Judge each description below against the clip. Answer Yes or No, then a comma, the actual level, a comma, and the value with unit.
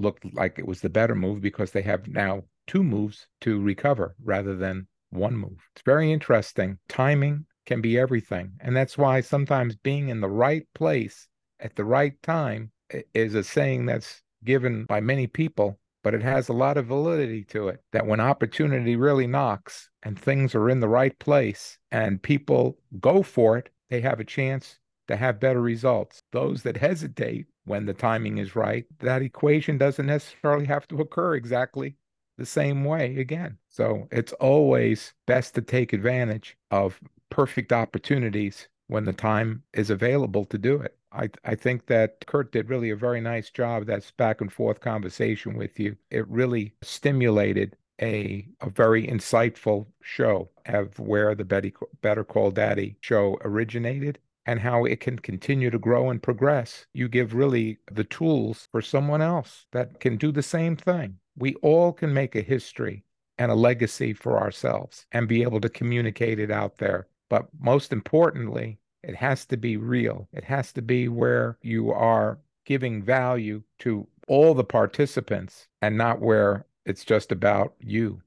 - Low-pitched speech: Yes, low, 120 Hz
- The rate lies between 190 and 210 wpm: No, average, 170 wpm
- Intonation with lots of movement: No, average, 4.1 semitones